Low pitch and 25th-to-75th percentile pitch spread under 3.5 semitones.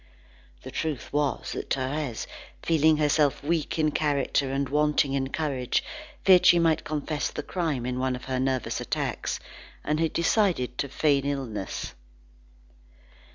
No: medium, 145 Hz; average, 2.8 semitones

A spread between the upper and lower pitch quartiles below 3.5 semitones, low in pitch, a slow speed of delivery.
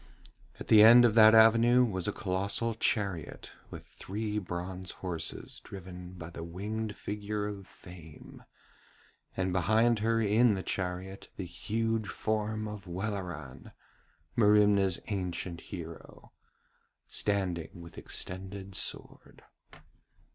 Yes: average, 3.1 semitones; low, 100 Hz; slow, 115 wpm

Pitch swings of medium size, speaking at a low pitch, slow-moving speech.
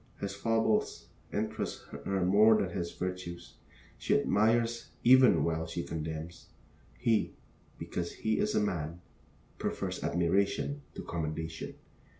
Yes: average, 4.6 semitones; very low, 90 Hz; slow, 120 wpm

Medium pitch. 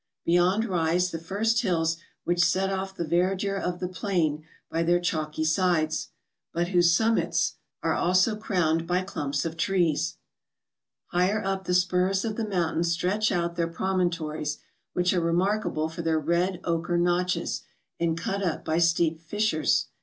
Yes: medium, 175 Hz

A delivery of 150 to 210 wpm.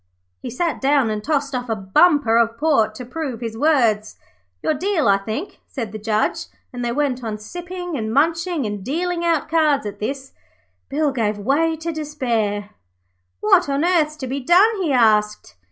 Yes: average, 180 wpm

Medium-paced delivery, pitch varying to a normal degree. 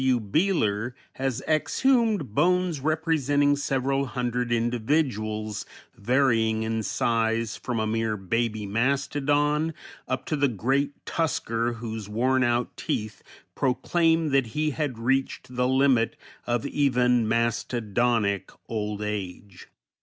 No: slow, 110 wpm; average, 4.1 semitones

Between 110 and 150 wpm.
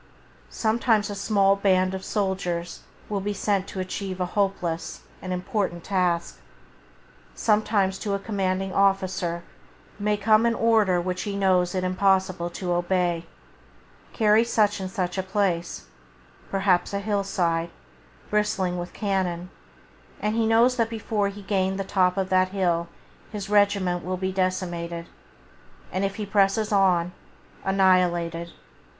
Yes: average, 145 wpm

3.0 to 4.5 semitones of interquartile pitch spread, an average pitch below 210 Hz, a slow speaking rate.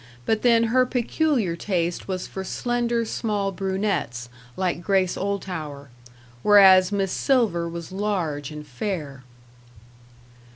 Yes: average, 4.1 semitones; high, 190 Hz; slow, 115 wpm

